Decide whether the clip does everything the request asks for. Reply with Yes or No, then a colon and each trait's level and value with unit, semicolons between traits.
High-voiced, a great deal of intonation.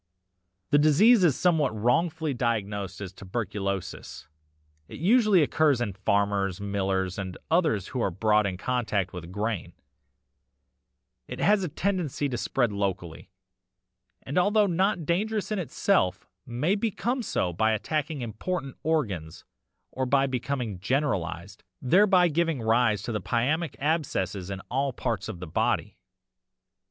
No: low, 125 Hz; wide, 8.5 semitones